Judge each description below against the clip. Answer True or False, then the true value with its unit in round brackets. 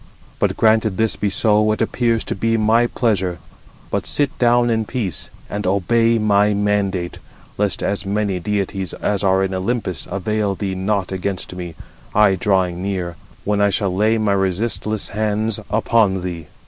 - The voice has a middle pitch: False (100 Hz)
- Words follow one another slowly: False (170 wpm)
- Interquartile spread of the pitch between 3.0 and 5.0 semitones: False (2.5 semitones)